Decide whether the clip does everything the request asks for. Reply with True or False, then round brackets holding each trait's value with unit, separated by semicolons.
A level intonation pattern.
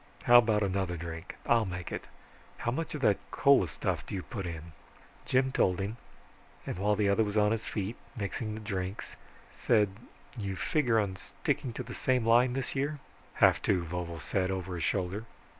False (4.1 semitones)